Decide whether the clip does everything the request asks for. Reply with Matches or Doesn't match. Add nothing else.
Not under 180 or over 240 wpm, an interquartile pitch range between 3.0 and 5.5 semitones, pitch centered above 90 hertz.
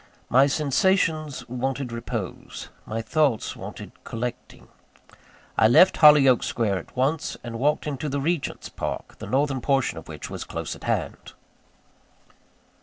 Doesn't match